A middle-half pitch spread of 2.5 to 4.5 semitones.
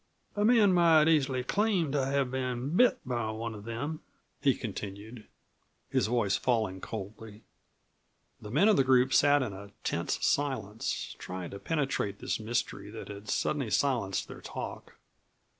No: average, 5.3 semitones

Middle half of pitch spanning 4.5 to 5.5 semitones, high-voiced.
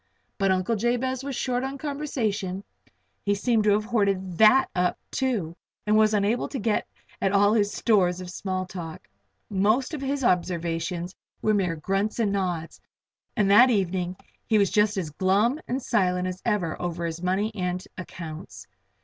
No: average, 3.9 semitones; high, 200 Hz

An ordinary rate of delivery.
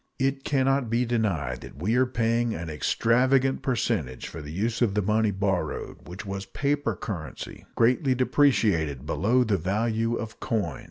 Yes: average, 165 wpm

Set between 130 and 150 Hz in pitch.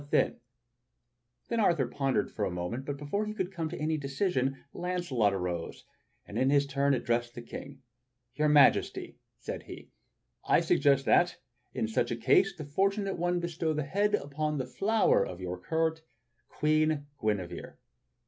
Yes: medium, 140 Hz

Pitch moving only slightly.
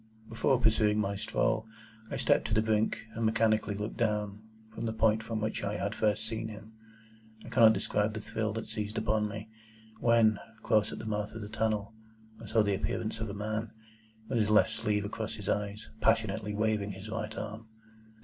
Yes: narrow, 1.1 semitones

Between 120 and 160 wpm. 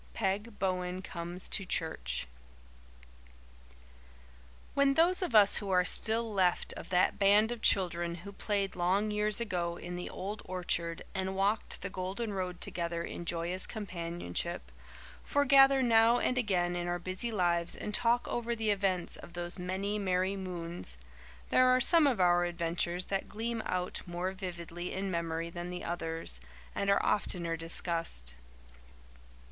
Yes: average, 150 wpm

